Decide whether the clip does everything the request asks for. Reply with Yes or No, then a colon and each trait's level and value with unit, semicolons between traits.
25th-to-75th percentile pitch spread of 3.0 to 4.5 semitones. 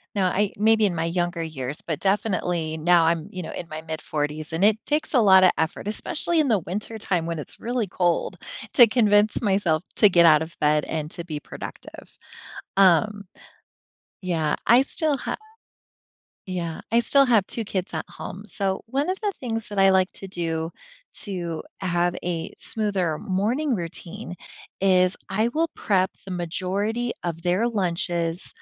Yes: average, 4.2 semitones